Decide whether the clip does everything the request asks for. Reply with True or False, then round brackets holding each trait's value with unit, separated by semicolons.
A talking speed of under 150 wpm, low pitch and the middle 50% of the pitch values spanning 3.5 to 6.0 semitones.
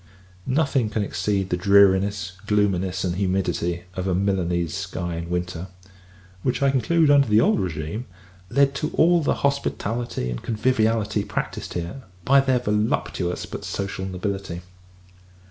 True (140 wpm; 100 Hz; 5.0 semitones)